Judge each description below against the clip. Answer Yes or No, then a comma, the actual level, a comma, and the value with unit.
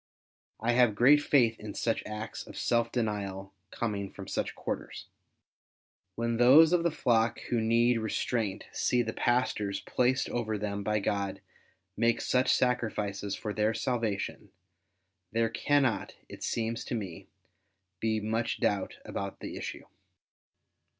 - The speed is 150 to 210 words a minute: No, slow, 135 wpm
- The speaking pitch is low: Yes, low, 115 Hz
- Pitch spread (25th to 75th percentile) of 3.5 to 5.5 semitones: No, average, 2.7 semitones